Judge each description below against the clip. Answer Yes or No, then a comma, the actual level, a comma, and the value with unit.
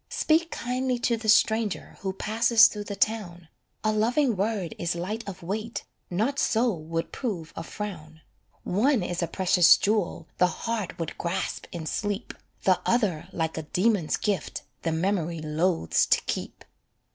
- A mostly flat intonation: No, average, 4.7 semitones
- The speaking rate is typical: Yes, average, 155 wpm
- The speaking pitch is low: No, high, 195 Hz